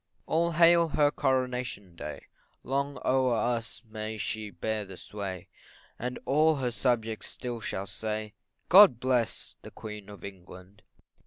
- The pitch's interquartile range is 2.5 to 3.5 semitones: No, average, 4.2 semitones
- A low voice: Yes, low, 115 Hz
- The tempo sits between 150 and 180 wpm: No, average, 140 wpm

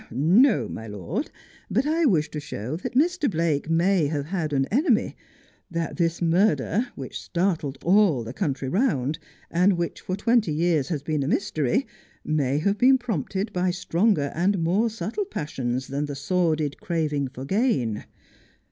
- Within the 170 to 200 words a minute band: No, average, 160 wpm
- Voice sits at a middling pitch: Yes, medium, 170 Hz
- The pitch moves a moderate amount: No, wide, 5.9 semitones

